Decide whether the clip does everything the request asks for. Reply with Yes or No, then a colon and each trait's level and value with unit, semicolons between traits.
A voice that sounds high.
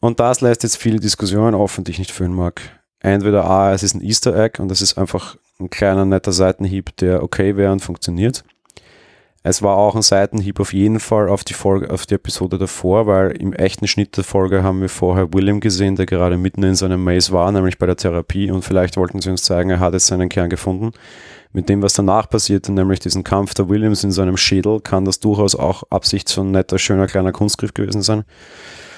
No: very low, 95 Hz